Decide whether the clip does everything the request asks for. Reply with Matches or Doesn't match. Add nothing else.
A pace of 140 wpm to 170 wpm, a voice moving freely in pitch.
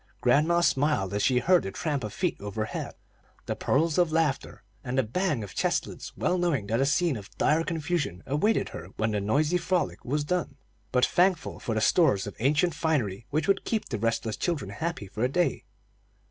Doesn't match